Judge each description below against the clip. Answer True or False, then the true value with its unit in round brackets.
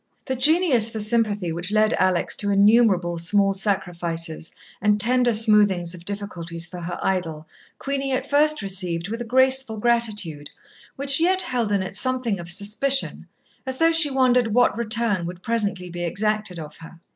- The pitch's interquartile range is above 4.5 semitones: True (5.5 semitones)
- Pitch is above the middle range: True (210 Hz)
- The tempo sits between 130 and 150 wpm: False (165 wpm)